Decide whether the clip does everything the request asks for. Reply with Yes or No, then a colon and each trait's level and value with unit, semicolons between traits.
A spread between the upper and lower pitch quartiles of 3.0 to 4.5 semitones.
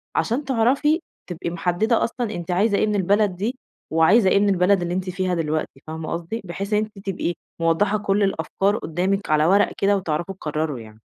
Yes: average, 3.6 semitones